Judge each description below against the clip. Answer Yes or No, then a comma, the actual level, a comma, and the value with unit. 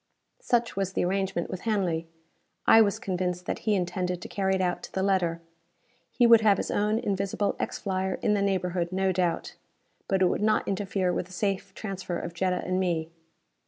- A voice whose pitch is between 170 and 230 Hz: Yes, high, 190 Hz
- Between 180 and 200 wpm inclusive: Yes, average, 195 wpm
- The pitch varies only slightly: Yes, narrow, 1.8 semitones